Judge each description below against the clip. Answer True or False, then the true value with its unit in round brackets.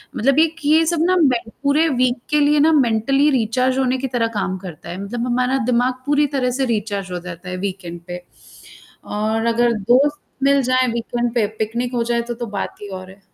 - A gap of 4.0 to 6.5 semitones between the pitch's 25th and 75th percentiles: True (4.6 semitones)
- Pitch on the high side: True (240 Hz)